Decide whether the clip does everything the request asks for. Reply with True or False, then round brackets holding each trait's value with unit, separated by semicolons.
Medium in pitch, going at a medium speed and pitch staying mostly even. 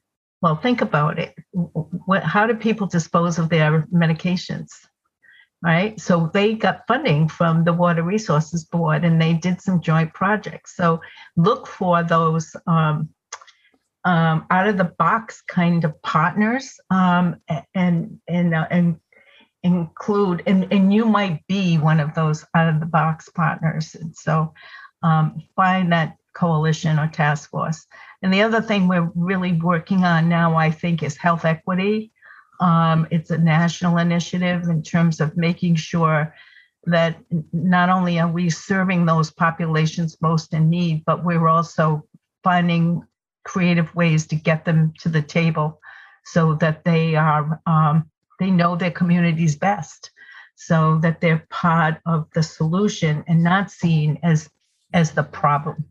True (170 Hz; 150 wpm; 2.1 semitones)